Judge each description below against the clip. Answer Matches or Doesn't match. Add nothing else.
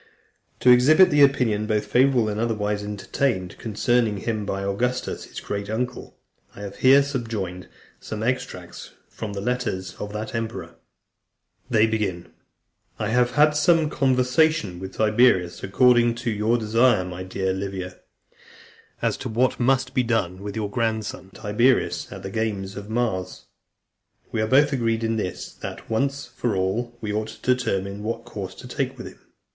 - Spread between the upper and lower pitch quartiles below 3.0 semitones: Doesn't match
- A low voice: Matches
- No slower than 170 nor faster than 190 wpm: Doesn't match